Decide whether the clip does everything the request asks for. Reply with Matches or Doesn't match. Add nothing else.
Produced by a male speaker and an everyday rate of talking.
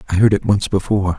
Doesn't match